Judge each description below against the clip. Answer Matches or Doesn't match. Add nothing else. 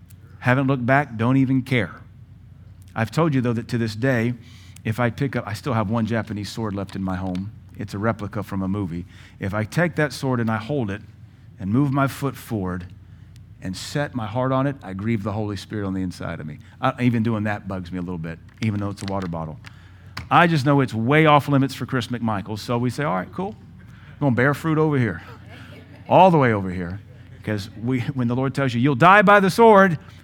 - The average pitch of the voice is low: Matches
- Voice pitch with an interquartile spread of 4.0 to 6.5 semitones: Matches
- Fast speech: Matches